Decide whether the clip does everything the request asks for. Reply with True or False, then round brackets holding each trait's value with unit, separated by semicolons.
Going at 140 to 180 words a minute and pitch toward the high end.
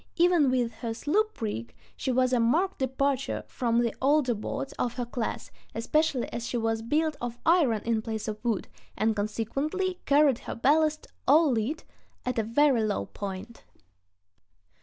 True (160 wpm; 245 Hz)